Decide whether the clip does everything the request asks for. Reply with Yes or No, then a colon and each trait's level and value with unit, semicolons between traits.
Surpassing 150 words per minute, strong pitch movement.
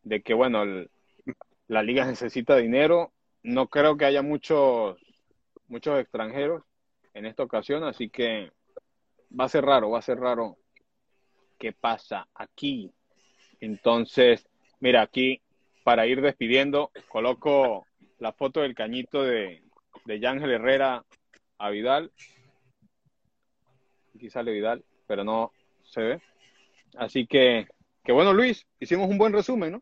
No: average, 130 wpm; wide, 7.3 semitones